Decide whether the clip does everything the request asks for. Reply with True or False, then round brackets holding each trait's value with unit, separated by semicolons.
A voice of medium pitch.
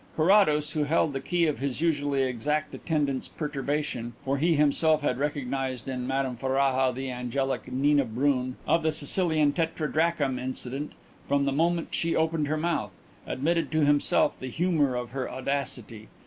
True (145 Hz)